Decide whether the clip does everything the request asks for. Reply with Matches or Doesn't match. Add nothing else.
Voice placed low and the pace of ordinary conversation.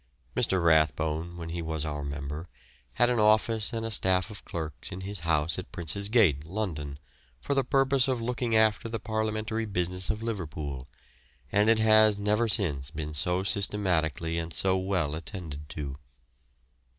Matches